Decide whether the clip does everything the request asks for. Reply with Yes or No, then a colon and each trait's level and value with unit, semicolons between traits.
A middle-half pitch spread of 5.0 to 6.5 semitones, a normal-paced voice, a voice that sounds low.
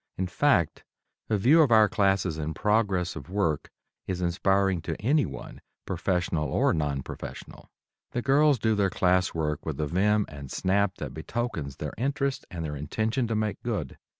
Yes: wide, 5.6 semitones; average, 170 wpm; very low, 95 Hz